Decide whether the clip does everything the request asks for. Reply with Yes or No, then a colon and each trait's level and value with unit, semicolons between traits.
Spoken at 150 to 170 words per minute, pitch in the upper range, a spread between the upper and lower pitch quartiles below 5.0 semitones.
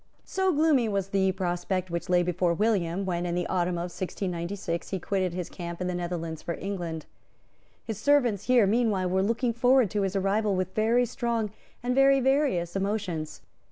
No: average, 180 wpm; high, 195 Hz; average, 4.3 semitones